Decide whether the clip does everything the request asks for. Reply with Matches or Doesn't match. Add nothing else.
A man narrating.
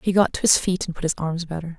Doesn't match